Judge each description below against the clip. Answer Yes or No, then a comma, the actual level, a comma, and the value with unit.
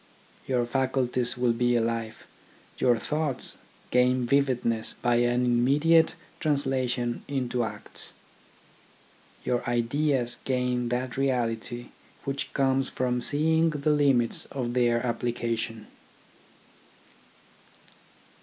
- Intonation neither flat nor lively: No, narrow, 2.1 semitones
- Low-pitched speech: Yes, low, 125 Hz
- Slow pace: Yes, slow, 100 wpm